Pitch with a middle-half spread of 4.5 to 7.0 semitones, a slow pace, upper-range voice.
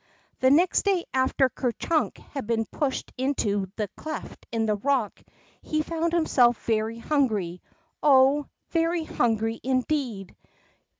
Yes: average, 5.3 semitones; slow, 130 wpm; very high, 260 Hz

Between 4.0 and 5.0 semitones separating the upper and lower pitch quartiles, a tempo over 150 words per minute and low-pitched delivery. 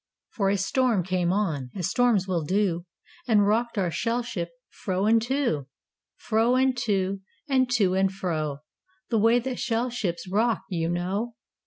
No: average, 4.5 semitones; average, 165 wpm; high, 200 Hz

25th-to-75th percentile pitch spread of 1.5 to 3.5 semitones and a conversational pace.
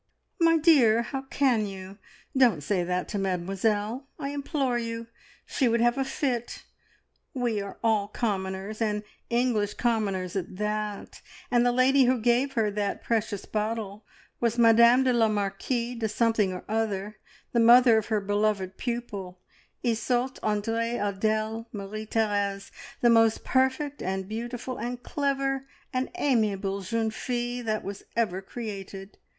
Yes: average, 3.0 semitones; average, 145 wpm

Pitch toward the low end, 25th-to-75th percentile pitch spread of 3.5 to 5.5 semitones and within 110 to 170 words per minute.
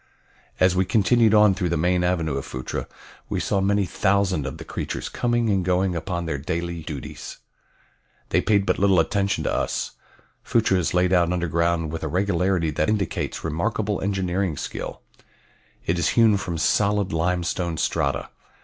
No: very low, 90 Hz; average, 3.0 semitones; average, 165 wpm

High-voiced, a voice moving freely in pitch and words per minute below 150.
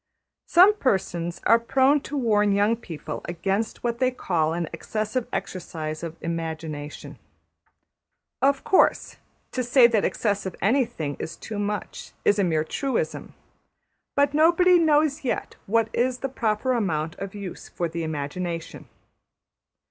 Yes: high, 210 Hz; wide, 7.4 semitones; average, 140 wpm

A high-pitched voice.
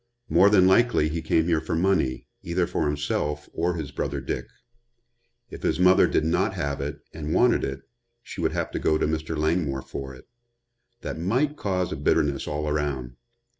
No: very low, 80 Hz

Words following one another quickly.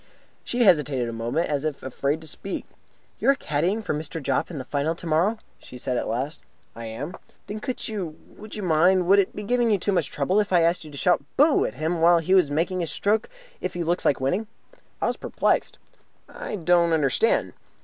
Yes: fast, 220 wpm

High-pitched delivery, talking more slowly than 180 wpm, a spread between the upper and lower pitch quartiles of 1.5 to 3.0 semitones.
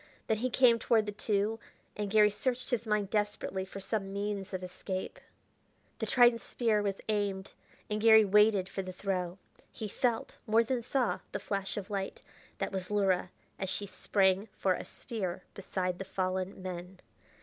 Yes: high, 205 Hz; average, 170 wpm; narrow, 2.5 semitones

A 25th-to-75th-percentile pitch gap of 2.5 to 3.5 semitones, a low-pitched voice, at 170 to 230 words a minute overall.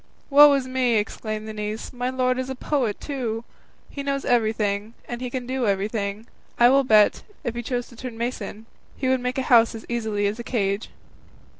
No: average, 2.9 semitones; high, 240 Hz; average, 200 wpm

